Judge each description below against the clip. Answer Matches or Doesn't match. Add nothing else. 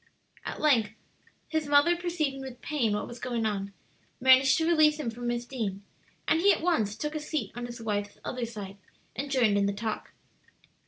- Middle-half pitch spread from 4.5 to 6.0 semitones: Matches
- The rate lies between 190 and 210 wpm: Matches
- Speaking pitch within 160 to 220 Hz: Doesn't match